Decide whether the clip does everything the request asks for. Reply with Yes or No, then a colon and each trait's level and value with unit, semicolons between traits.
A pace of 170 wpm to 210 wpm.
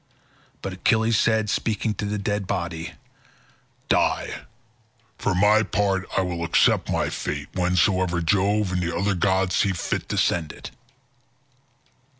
No: average, 140 wpm